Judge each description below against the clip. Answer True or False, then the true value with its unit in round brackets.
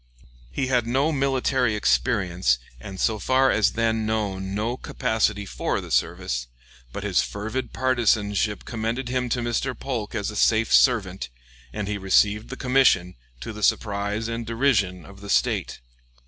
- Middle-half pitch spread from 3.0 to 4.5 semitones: True (3.5 semitones)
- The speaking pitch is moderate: False (110 Hz)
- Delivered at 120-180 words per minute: True (155 wpm)